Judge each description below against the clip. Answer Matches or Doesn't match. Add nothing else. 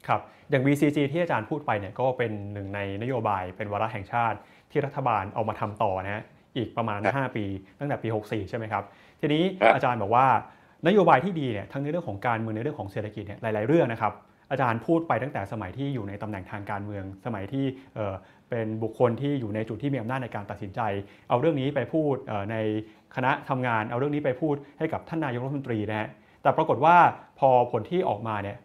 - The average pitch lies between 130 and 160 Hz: Doesn't match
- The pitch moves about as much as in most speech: Matches